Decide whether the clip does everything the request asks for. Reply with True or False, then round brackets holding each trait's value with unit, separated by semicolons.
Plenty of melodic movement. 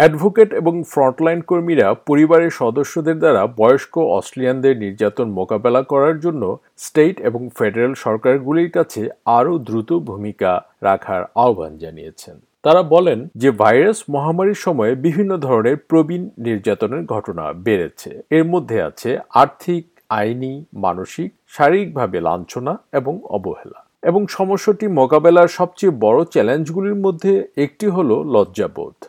True (5.7 semitones)